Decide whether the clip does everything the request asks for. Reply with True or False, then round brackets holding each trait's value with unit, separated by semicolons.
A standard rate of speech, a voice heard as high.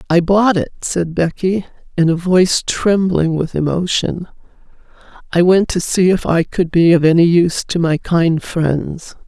False (170 wpm; 175 Hz)